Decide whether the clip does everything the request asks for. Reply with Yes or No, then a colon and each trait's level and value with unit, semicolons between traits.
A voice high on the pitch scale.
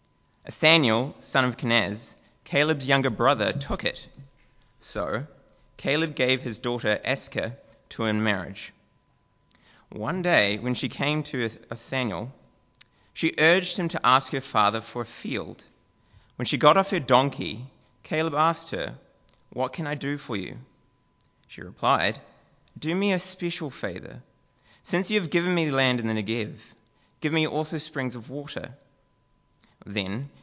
No: low, 135 Hz